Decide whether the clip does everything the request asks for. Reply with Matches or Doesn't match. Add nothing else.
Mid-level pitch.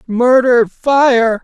Doesn't match